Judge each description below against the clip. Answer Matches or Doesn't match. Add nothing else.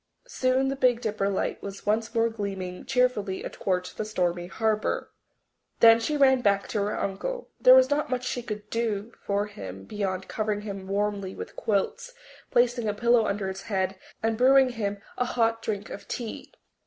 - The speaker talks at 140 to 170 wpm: Doesn't match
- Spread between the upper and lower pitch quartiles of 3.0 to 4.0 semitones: Matches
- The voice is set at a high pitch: Matches